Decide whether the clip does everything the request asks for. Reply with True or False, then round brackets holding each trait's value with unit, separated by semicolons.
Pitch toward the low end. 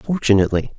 True (110 Hz)